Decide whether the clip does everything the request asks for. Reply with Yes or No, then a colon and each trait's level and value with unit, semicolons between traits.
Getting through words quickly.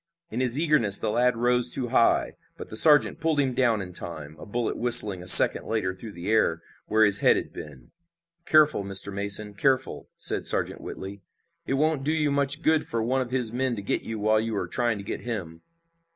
Yes: fast, 215 wpm